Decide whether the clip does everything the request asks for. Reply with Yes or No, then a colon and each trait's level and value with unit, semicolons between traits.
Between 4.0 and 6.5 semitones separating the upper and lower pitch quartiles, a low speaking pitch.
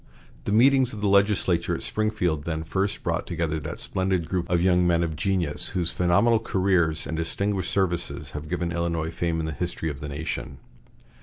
No: average, 3.2 semitones; very low, 85 Hz